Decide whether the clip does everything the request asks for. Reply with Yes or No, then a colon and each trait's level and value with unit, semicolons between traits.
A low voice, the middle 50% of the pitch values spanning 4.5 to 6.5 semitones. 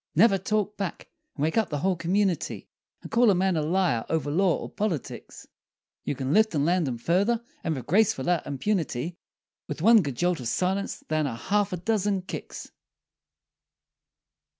No: medium, 180 Hz; average, 5.1 semitones